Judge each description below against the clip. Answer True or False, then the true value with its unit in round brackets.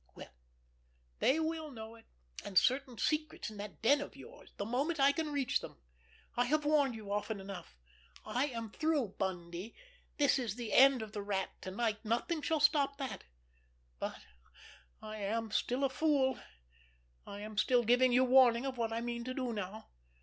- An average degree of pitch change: True (4.9 semitones)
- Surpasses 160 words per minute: True (180 wpm)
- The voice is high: True (240 Hz)